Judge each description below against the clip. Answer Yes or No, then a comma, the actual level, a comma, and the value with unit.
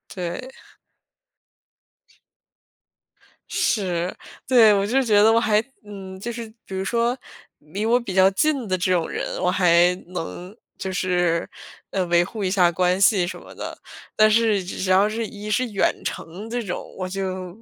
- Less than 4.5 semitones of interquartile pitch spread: Yes, average, 3.2 semitones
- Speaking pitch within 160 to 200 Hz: Yes, high, 195 Hz